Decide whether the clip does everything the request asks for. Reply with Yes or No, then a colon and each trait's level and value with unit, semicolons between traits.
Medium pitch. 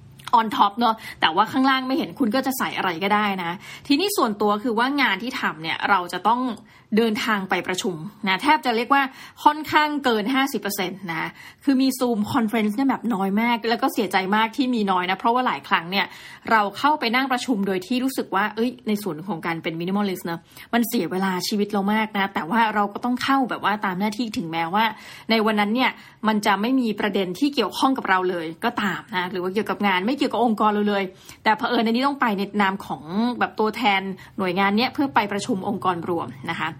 No: high, 220 Hz